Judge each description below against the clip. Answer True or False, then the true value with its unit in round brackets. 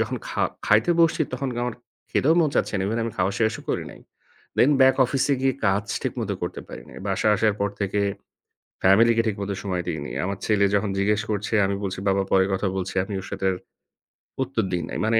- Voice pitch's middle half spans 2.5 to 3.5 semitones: True (2.9 semitones)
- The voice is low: True (105 Hz)